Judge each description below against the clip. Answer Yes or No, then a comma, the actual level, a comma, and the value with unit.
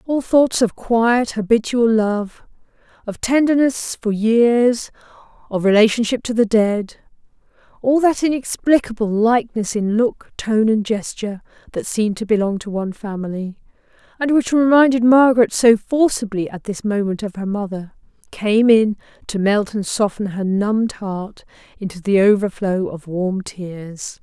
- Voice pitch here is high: Yes, high, 215 Hz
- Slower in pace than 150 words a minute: Yes, average, 140 wpm